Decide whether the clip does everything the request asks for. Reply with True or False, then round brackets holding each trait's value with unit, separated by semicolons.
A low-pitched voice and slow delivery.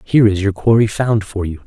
False (105 Hz; 250 wpm)